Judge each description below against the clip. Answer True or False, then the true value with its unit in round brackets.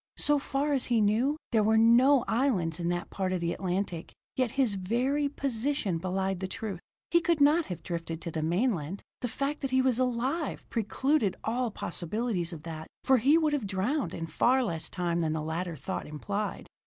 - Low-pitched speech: False (220 Hz)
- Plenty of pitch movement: True (7.1 semitones)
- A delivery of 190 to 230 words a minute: True (195 wpm)